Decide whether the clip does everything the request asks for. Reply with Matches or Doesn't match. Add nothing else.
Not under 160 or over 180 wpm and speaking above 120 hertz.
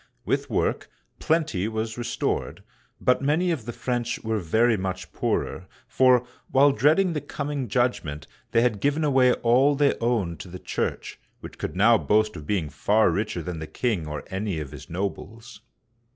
Doesn't match